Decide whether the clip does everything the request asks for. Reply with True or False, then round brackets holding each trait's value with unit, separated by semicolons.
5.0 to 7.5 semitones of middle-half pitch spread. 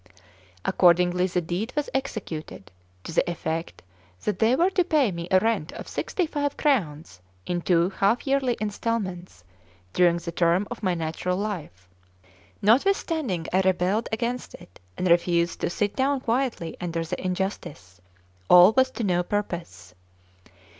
True (5.5 semitones)